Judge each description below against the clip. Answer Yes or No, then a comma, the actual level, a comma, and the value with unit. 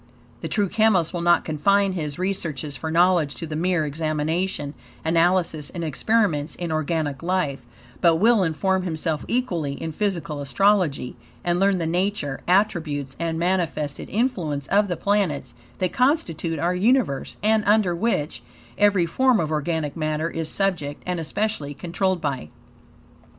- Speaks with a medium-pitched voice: Yes, medium, 170 Hz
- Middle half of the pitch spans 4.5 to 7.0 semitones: No, average, 4.1 semitones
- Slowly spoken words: No, average, 145 wpm